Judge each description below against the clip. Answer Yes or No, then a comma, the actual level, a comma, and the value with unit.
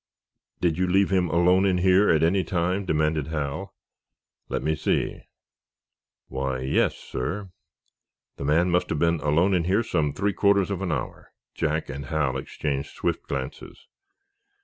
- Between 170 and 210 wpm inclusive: No, average, 155 wpm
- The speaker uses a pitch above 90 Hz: No, very low, 85 Hz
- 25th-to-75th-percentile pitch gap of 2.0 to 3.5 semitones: No, average, 3.9 semitones